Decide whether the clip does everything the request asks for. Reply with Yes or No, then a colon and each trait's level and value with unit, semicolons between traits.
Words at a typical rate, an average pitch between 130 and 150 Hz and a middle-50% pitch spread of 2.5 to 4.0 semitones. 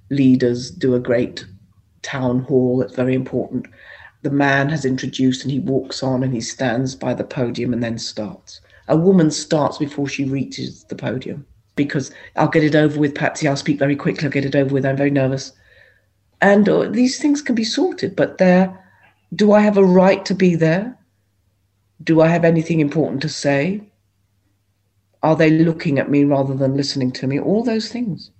No: average, 190 wpm; medium, 140 Hz; average, 4.5 semitones